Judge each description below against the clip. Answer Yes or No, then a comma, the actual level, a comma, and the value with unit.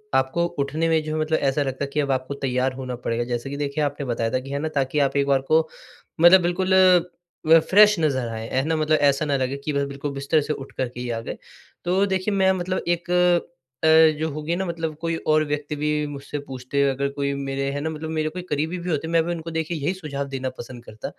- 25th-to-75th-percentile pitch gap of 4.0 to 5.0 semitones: No, average, 3.3 semitones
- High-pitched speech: No, medium, 150 Hz